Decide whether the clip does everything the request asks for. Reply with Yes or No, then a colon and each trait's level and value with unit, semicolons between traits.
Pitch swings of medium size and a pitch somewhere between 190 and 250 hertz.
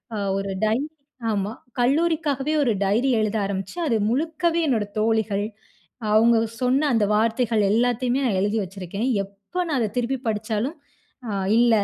Yes: average, 4.2 semitones; high, 230 Hz